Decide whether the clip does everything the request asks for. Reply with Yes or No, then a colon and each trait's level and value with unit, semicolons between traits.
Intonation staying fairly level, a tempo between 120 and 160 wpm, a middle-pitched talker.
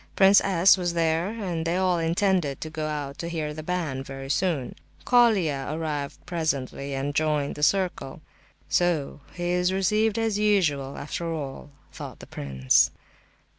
No: average, 4.3 semitones; average, 155 wpm; medium, 165 Hz